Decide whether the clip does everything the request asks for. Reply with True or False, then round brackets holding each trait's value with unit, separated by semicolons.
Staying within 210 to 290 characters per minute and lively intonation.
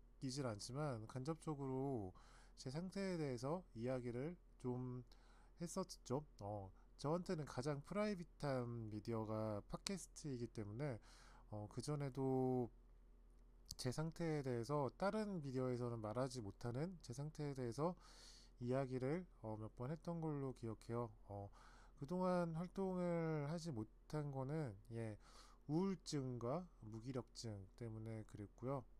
True (265 characters per minute; 5.7 semitones)